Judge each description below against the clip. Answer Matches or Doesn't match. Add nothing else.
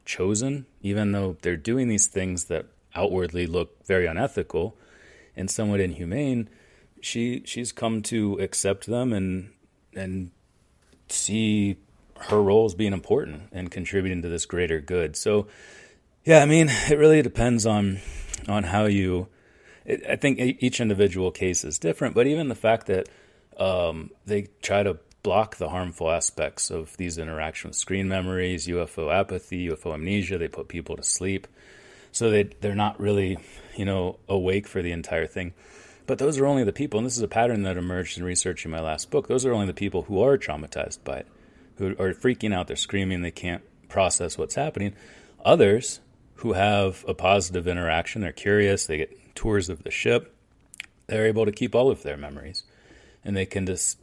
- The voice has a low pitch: Matches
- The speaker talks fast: Doesn't match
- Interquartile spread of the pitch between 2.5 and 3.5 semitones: Matches